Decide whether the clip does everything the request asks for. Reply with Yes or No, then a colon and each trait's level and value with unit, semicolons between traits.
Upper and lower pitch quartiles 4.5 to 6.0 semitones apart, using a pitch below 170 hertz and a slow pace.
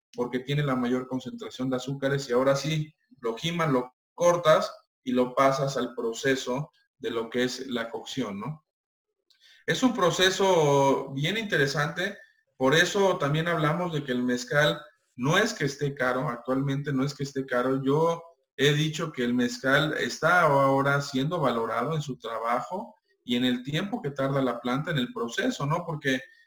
No: average, 4.8 semitones; medium, 140 Hz; average, 170 wpm